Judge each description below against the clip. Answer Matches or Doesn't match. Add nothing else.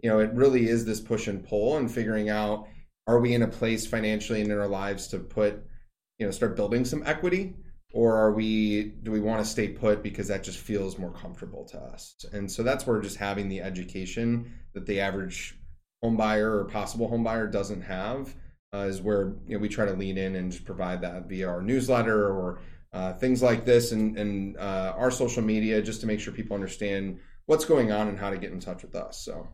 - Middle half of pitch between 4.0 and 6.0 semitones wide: Doesn't match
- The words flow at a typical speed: Doesn't match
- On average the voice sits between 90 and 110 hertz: Matches